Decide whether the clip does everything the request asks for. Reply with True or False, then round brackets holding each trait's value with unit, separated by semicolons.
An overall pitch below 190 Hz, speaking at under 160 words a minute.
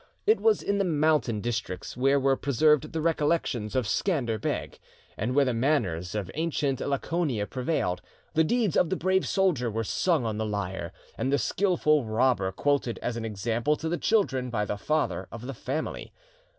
False (135 Hz; 180 wpm)